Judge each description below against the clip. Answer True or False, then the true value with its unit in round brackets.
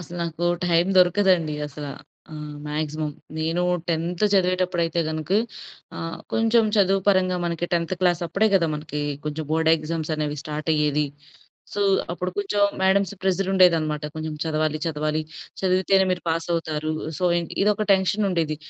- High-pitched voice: False (170 Hz)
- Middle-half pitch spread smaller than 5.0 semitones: True (3.2 semitones)